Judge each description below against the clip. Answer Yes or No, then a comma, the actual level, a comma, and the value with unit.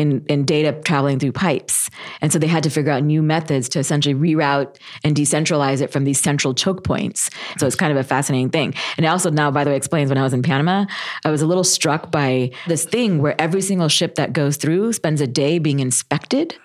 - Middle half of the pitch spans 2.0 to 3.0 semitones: Yes, narrow, 2.6 semitones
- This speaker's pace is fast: Yes, fast, 240 wpm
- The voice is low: No, medium, 150 Hz